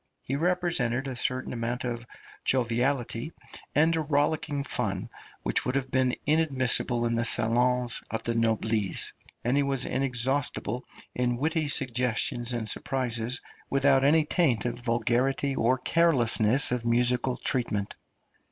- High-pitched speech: No, low, 125 Hz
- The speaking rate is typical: No, slow, 130 wpm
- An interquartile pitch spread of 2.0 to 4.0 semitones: Yes, average, 2.8 semitones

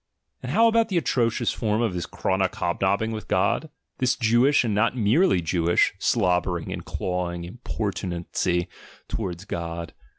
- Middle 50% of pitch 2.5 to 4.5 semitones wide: No, average, 5.2 semitones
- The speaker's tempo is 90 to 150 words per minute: Yes, average, 140 wpm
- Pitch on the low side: Yes, low, 100 Hz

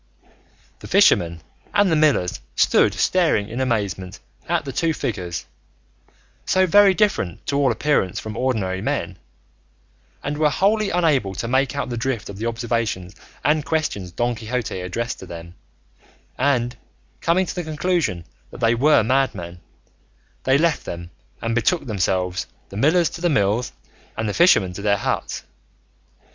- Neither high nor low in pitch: No, low, 120 Hz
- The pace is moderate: Yes, average, 155 wpm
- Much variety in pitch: Yes, wide, 7.9 semitones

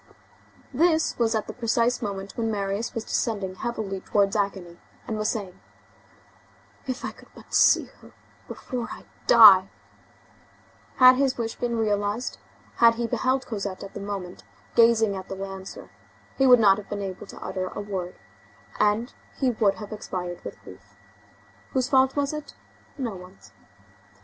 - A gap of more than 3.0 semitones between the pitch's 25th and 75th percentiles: Yes, average, 3.6 semitones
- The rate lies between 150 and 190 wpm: Yes, average, 155 wpm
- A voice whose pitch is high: Yes, high, 215 Hz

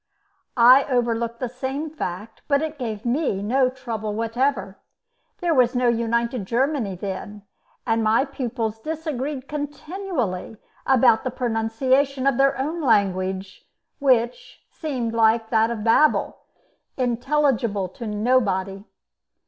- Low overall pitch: No, high, 240 Hz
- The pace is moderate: No, slow, 120 wpm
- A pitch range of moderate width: Yes, average, 3.6 semitones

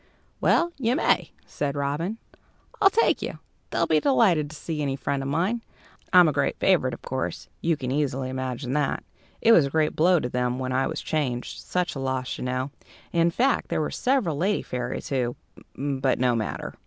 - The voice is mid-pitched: Yes, medium, 145 Hz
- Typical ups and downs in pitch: Yes, average, 4.9 semitones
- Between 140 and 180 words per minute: No, average, 195 wpm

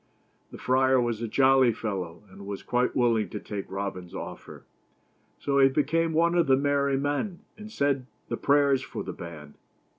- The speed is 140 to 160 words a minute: No, average, 175 wpm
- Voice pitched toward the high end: No, low, 130 Hz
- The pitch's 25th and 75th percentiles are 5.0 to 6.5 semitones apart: Yes, wide, 5.4 semitones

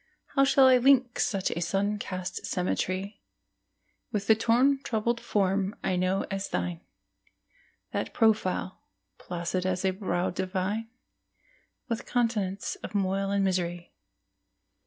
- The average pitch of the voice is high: Yes, high, 195 Hz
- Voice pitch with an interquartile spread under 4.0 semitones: Yes, average, 3.4 semitones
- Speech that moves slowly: Yes, slow, 120 wpm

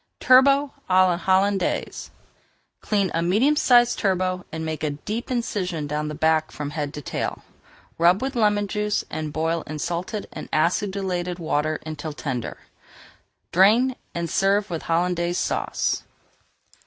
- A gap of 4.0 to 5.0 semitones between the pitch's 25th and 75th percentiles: Yes, average, 4.6 semitones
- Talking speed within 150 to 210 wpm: No, average, 140 wpm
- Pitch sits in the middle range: Yes, medium, 180 Hz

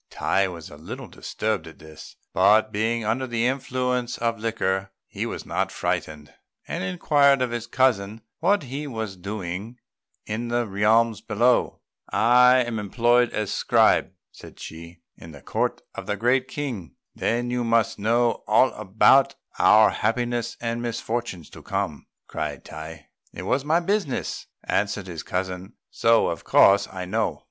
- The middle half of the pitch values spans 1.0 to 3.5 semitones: No, average, 4.0 semitones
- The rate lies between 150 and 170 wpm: Yes, average, 155 wpm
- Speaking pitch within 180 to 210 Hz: No, low, 115 Hz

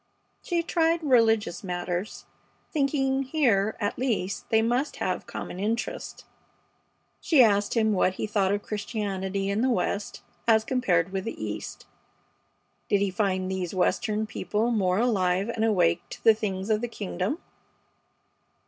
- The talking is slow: No, average, 150 wpm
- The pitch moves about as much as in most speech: Yes, average, 3.7 semitones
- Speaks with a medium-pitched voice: No, high, 210 Hz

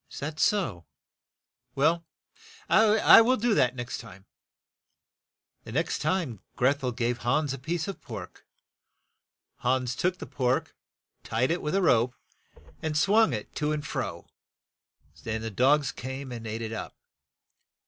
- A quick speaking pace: No, average, 155 wpm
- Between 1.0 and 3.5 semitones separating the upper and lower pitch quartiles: No, wide, 5.4 semitones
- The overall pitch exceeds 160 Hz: No, low, 135 Hz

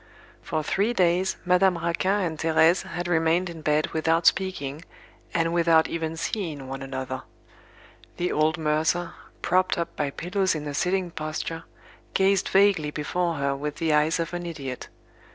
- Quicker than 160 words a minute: No, average, 155 wpm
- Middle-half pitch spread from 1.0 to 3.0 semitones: Yes, narrow, 2.6 semitones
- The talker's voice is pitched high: No, medium, 165 Hz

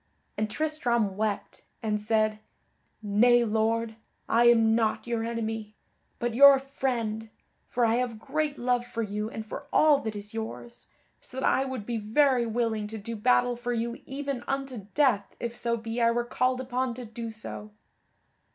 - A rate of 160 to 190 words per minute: Yes, average, 170 wpm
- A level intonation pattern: Yes, narrow, 2.3 semitones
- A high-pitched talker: Yes, high, 235 Hz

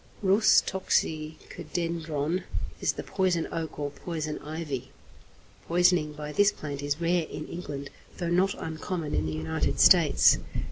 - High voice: No, medium, 160 Hz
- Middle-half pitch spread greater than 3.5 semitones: No, average, 3.0 semitones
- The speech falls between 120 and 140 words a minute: Yes, slow, 135 wpm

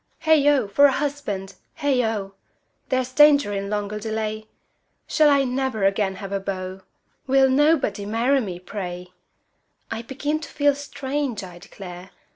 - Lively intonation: Yes, wide, 6.1 semitones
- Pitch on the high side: Yes, high, 225 Hz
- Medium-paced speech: Yes, average, 150 wpm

